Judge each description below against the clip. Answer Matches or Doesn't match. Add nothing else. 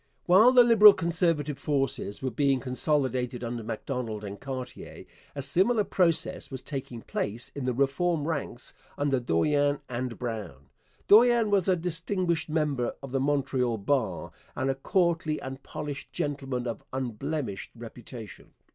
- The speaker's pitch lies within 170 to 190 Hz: Doesn't match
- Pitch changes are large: Doesn't match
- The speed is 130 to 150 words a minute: Matches